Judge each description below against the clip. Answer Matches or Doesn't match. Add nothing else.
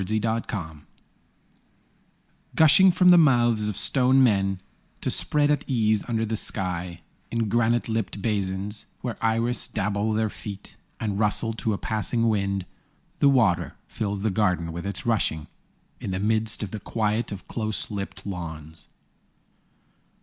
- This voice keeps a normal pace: Matches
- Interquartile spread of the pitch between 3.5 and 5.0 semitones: Doesn't match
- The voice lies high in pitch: Doesn't match